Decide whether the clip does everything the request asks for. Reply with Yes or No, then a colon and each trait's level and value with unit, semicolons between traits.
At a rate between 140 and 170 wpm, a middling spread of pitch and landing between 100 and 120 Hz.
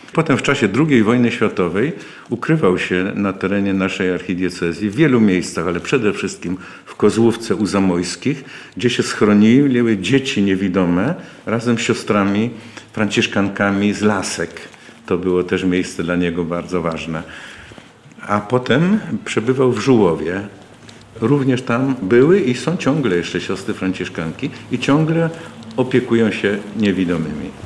No: average, 130 wpm; average, 4.7 semitones; low, 105 Hz